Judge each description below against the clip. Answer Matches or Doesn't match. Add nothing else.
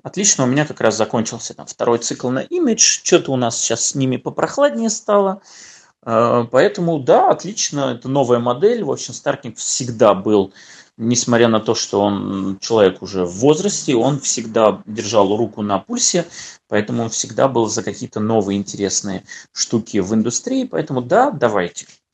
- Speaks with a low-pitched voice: Matches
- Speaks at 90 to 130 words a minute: Doesn't match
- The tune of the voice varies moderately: Doesn't match